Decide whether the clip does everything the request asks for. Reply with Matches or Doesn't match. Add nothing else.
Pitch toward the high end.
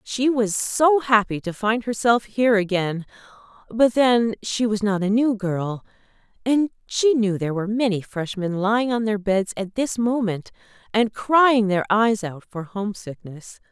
Matches